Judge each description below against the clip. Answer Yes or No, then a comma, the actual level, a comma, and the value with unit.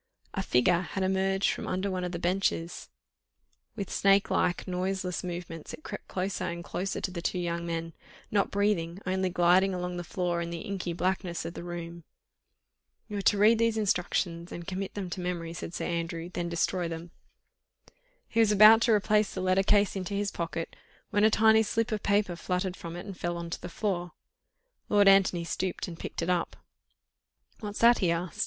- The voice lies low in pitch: No, medium, 180 Hz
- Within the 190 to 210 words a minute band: Yes, average, 195 wpm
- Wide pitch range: No, narrow, 2.5 semitones